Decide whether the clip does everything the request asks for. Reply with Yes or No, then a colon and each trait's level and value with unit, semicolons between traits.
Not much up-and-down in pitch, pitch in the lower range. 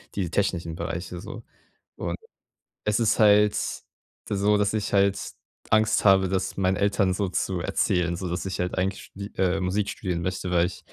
Yes: narrow, 2.1 semitones; very low, 95 Hz